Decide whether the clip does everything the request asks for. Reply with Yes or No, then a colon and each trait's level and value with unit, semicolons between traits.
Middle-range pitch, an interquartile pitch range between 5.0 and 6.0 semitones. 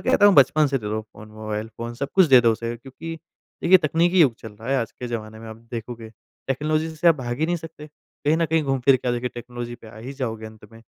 No: low, 125 Hz; average, 5.3 semitones